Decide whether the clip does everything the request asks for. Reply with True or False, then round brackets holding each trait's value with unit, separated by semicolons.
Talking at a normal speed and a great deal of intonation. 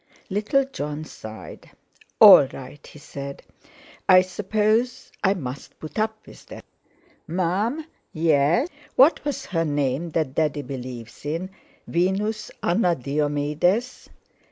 False (115 wpm; 6.5 semitones)